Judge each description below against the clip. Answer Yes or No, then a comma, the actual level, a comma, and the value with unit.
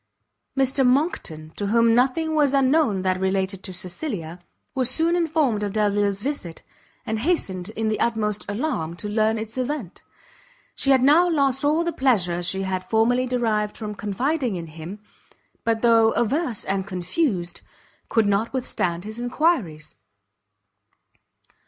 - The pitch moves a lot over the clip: Yes, wide, 5.8 semitones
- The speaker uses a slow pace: No, average, 145 wpm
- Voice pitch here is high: Yes, high, 220 Hz